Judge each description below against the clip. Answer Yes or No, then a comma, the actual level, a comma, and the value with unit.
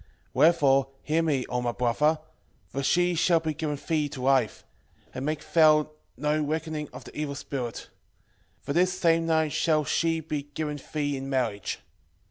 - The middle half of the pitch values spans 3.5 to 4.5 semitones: No, average, 2.7 semitones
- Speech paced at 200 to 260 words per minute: No, average, 165 wpm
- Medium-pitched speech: Yes, medium, 150 Hz